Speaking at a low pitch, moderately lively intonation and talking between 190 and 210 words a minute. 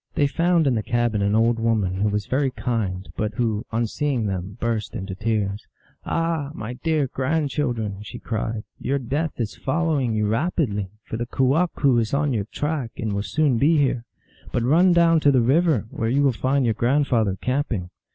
Yes: low, 120 Hz; average, 4.9 semitones; average, 200 wpm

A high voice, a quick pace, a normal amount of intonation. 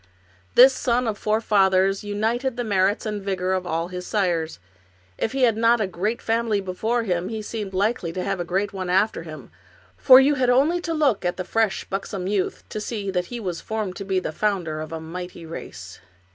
Yes: high, 200 Hz; fast, 220 wpm; average, 3.8 semitones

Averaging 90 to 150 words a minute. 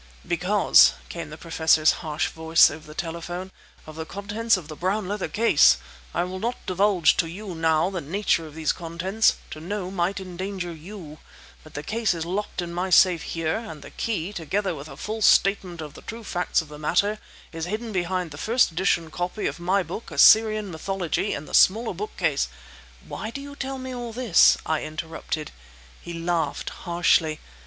No: average, 185 wpm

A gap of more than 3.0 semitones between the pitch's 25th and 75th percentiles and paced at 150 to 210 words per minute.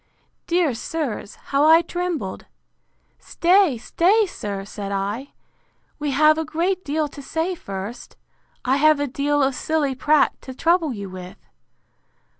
No: average, 5.2 semitones; average, 140 wpm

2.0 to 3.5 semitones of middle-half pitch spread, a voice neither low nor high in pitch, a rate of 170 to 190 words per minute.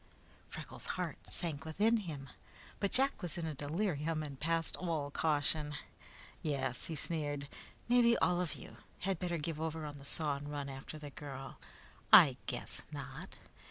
No: average, 3.0 semitones; medium, 155 Hz; average, 160 wpm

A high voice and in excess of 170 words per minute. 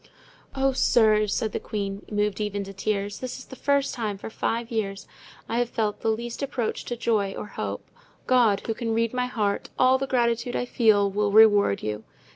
Yes: high, 220 Hz; average, 200 wpm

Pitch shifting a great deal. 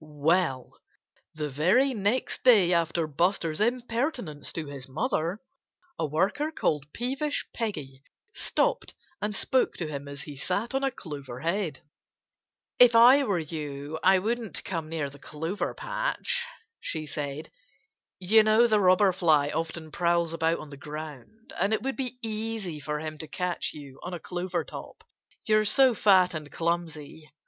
Yes: wide, 6.3 semitones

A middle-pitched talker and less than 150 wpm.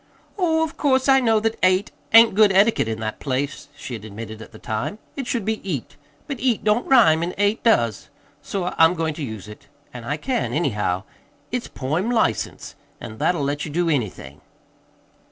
No: medium, 170 Hz; average, 190 wpm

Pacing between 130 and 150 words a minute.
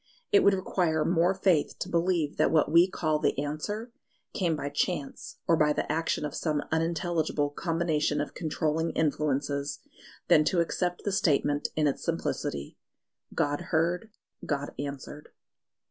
Yes: average, 145 wpm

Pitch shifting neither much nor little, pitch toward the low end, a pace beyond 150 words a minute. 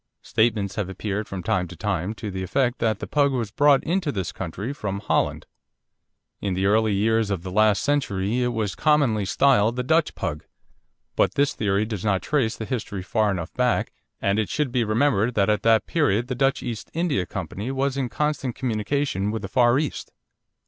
Yes: average, 5.0 semitones; low, 110 Hz; average, 195 wpm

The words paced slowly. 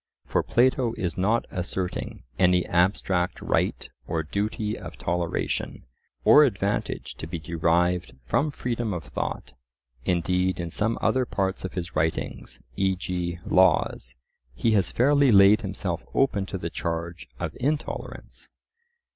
Yes: slow, 130 wpm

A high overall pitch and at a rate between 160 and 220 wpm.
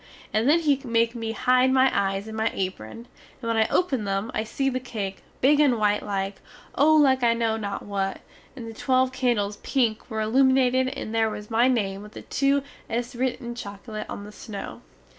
Yes: high, 230 Hz; fast, 205 wpm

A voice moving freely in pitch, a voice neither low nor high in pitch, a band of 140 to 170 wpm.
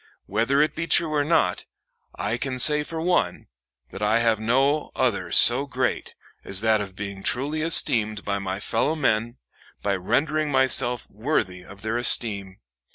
No: wide, 5.9 semitones; low, 120 Hz; average, 160 wpm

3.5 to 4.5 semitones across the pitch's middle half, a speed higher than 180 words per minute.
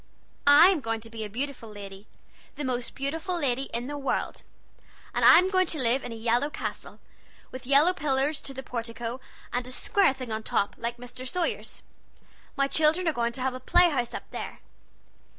Yes: average, 3.9 semitones; average, 190 wpm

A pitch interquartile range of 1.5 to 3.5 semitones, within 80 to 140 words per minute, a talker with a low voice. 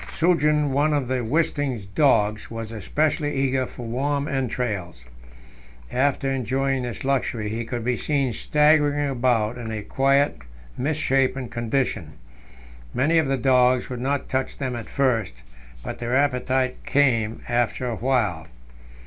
Yes: average, 3.1 semitones; slow, 135 wpm; low, 130 Hz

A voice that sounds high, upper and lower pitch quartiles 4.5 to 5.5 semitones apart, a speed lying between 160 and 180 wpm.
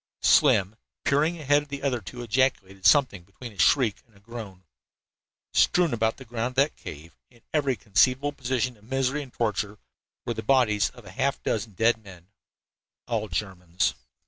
No: low, 115 Hz; average, 4.8 semitones; average, 170 wpm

